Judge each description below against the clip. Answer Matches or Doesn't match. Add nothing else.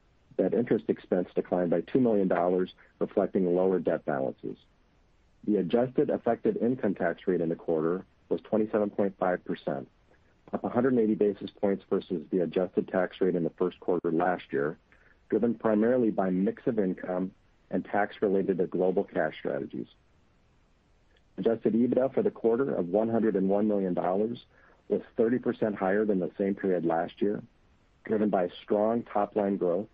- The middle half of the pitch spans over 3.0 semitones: Doesn't match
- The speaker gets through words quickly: Doesn't match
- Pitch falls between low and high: Doesn't match